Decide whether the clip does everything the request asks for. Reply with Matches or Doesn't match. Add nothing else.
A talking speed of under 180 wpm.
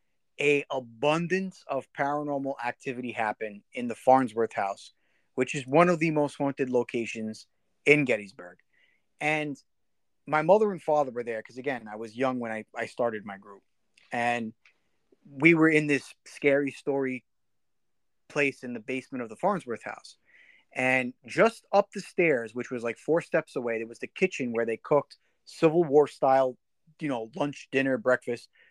Matches